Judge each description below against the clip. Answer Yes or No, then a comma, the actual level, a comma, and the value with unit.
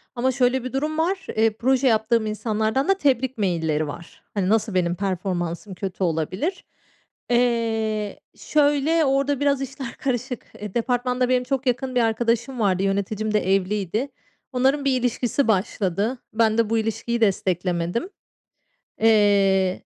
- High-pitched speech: Yes, high, 225 Hz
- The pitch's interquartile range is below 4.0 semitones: No, average, 4.7 semitones